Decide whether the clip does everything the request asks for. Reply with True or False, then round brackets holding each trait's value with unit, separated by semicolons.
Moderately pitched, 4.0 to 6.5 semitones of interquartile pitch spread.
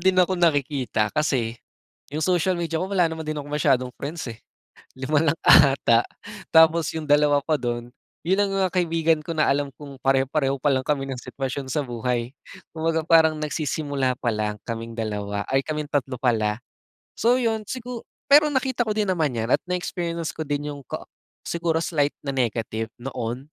True (145 Hz; 4.5 semitones)